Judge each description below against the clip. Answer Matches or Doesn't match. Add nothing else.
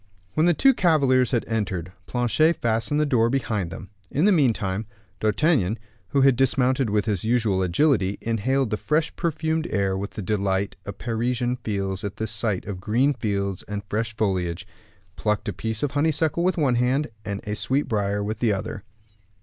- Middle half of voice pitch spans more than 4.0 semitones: Matches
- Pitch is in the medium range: Doesn't match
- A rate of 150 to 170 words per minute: Doesn't match